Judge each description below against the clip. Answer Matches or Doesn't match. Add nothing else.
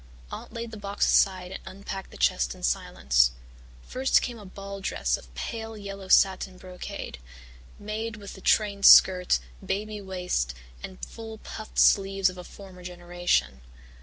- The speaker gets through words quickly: Doesn't match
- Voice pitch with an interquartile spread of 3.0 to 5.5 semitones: Doesn't match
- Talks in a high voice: Matches